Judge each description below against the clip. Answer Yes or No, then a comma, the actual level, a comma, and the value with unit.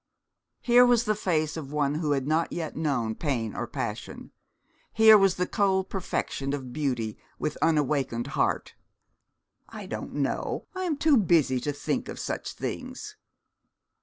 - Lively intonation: Yes, wide, 6.1 semitones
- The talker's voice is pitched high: No, medium, 155 Hz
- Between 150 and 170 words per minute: Yes, average, 155 wpm